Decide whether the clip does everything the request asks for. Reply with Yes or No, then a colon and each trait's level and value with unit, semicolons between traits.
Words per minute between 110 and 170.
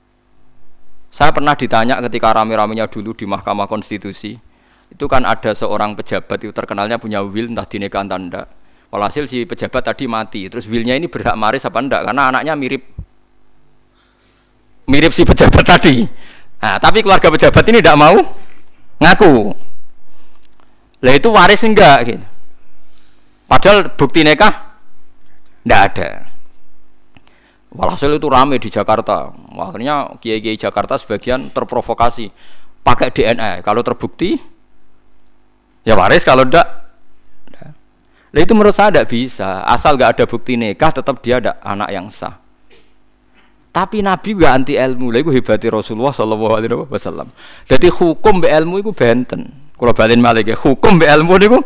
Yes: average, 135 wpm